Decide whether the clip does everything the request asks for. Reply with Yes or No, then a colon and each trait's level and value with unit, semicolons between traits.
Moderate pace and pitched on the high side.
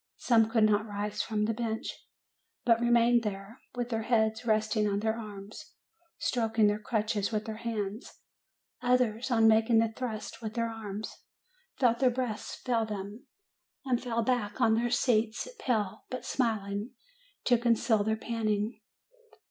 Yes: average, 150 wpm; high, 225 Hz